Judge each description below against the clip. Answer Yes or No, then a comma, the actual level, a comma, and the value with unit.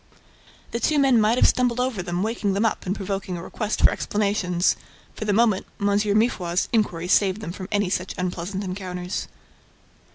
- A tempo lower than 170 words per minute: No, average, 175 wpm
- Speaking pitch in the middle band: No, high, 200 Hz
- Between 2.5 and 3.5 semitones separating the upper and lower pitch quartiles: Yes, average, 3.0 semitones